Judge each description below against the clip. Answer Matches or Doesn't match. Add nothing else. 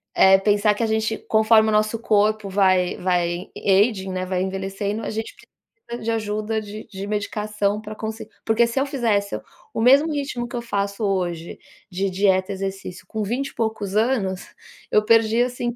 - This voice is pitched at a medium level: Doesn't match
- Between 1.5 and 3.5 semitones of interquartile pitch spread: Matches